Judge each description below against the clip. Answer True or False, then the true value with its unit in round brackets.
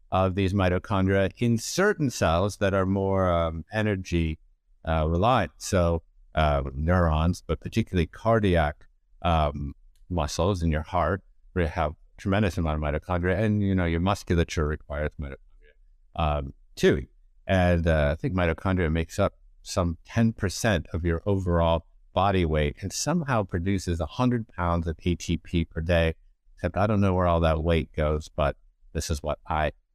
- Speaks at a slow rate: False (160 wpm)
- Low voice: True (85 Hz)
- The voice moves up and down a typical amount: True (3.3 semitones)